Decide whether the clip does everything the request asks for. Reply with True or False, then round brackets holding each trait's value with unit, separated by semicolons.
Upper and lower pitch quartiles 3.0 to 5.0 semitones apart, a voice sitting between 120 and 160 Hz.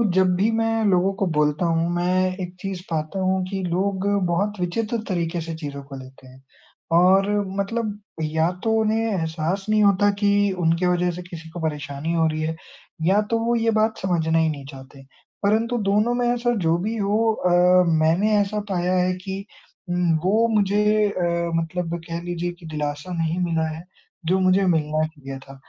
False (3.8 semitones; 180 Hz)